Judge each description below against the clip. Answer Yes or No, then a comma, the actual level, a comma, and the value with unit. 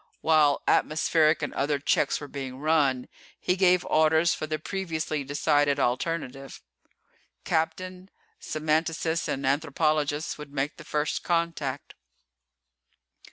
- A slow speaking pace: Yes, slow, 115 wpm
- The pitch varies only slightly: Yes, narrow, 2.2 semitones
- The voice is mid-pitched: Yes, medium, 155 Hz